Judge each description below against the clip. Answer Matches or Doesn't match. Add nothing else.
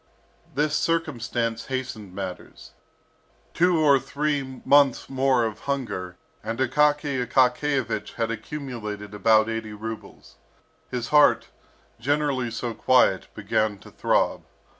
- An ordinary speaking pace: Doesn't match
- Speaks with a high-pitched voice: Doesn't match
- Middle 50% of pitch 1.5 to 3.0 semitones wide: Doesn't match